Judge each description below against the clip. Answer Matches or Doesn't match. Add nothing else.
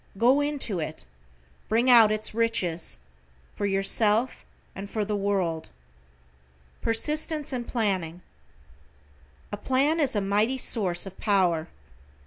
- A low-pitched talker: Doesn't match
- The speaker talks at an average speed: Doesn't match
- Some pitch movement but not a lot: Matches